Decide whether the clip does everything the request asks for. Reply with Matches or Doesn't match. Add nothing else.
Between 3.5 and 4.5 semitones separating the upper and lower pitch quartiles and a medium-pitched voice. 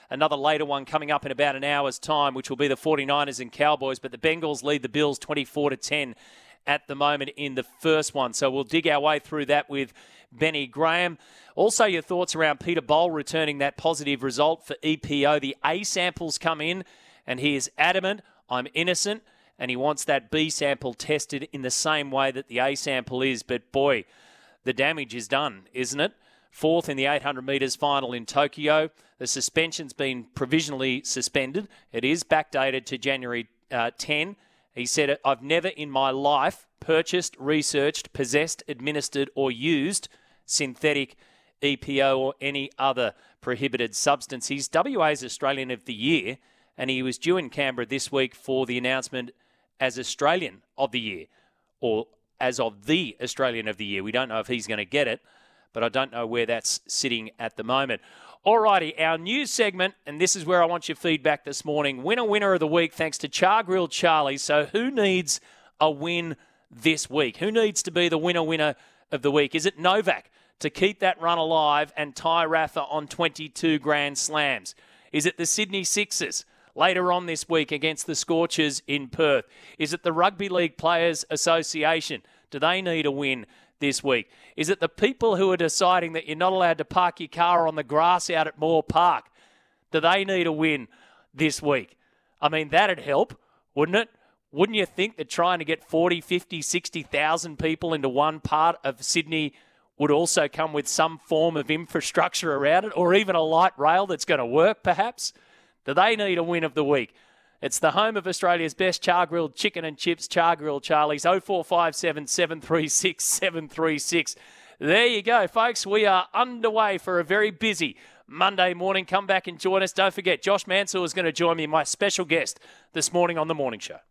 Matches